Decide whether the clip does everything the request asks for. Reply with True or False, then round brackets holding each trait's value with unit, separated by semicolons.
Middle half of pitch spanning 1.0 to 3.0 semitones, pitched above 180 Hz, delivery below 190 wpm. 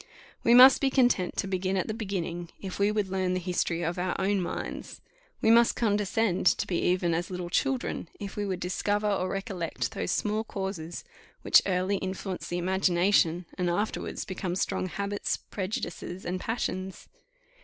True (2.4 semitones; 190 Hz; 170 wpm)